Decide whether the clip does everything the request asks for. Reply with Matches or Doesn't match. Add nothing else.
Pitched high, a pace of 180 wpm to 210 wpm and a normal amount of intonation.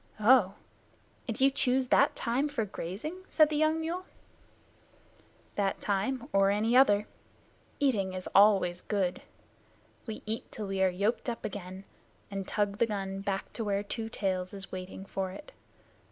Doesn't match